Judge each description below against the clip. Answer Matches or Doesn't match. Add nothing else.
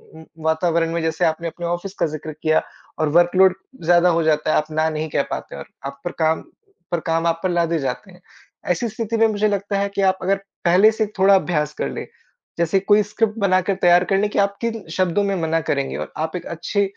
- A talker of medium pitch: Matches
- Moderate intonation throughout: Matches